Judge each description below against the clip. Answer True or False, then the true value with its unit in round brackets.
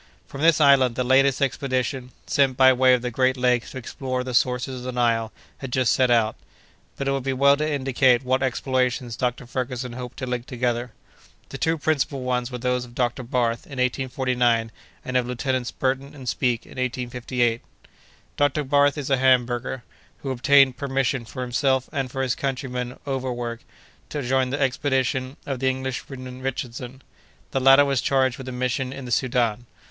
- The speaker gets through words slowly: False (185 wpm)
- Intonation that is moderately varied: False (1.4 semitones)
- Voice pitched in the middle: False (130 Hz)